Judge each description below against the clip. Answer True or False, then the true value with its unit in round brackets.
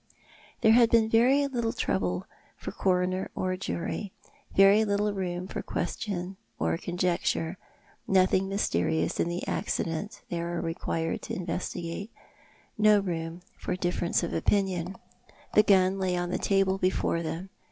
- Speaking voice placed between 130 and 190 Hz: True (185 Hz)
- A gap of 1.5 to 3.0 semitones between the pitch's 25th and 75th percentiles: True (2.7 semitones)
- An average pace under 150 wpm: True (140 wpm)